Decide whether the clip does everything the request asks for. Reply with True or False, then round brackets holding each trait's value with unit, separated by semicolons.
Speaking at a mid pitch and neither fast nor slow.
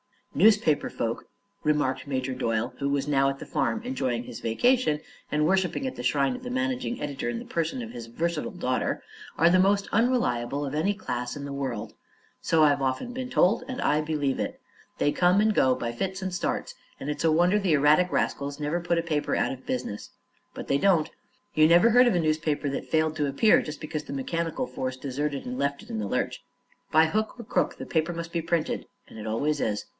False (155 Hz; 220 wpm)